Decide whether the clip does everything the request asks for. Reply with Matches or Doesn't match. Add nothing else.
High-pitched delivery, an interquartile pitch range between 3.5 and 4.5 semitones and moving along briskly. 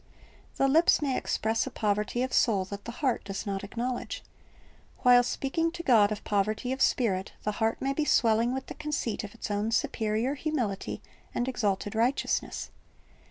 Doesn't match